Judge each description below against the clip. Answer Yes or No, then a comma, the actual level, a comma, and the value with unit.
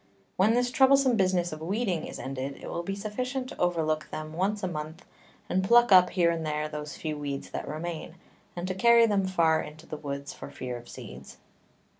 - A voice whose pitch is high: No, medium, 175 Hz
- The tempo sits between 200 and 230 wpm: Yes, fast, 205 wpm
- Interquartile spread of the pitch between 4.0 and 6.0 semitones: Yes, average, 4.7 semitones